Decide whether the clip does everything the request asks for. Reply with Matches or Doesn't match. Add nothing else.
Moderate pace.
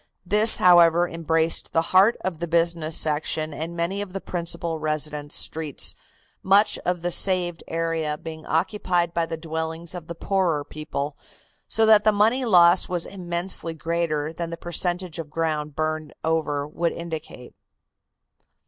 Matches